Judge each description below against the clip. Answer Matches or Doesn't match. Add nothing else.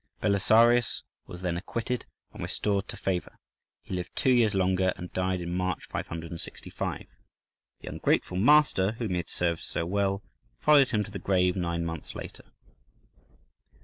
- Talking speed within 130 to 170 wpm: Matches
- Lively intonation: Doesn't match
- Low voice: Matches